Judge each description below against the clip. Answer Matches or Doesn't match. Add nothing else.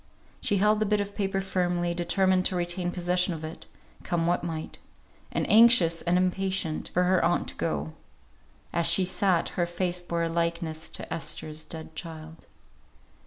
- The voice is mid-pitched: Matches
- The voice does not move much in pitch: Matches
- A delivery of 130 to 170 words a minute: Matches